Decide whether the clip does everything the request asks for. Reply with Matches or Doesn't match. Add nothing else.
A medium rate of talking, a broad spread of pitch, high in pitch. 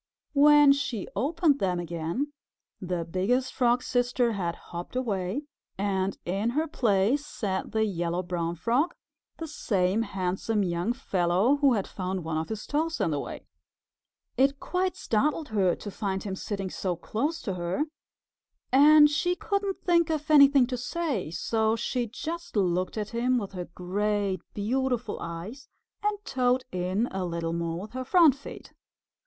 Matches